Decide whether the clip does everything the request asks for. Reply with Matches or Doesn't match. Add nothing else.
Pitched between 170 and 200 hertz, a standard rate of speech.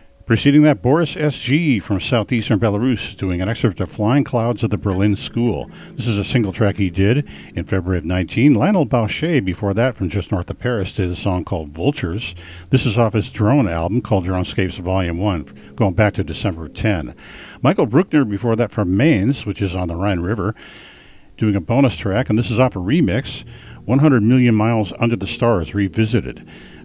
Doesn't match